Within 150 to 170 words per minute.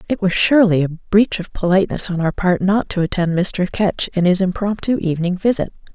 No: average, 200 wpm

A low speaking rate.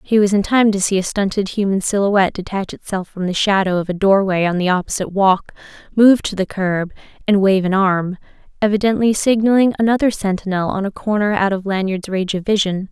No: average, 195 wpm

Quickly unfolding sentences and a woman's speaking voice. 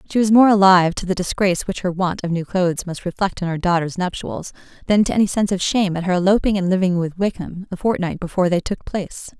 Yes: fast, 245 wpm; female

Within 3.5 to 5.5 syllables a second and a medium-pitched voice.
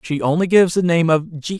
No: 6.0 syllables/s; medium, 165 Hz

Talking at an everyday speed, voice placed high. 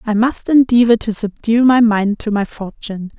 Yes: average, 190 wpm; high, 225 Hz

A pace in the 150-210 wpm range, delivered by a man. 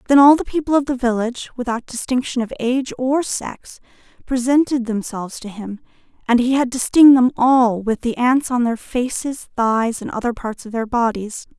No: average, 190 wpm; female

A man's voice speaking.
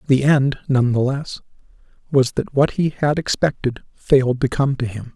Yes: male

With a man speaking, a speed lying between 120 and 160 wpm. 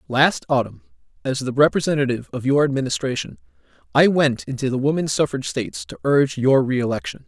Yes: male; average, 155 wpm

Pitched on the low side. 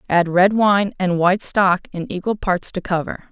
No: medium, 185 Hz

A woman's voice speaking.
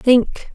Yes: female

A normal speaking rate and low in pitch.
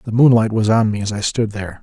No: fast, 295 wpm; low, 110 Hz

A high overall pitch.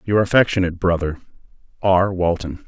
No: very low, 90 Hz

